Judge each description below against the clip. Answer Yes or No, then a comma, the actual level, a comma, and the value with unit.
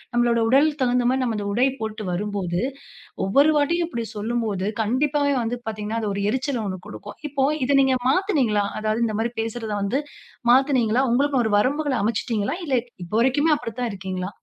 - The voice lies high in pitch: Yes, high, 235 Hz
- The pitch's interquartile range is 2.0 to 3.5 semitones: No, average, 4.2 semitones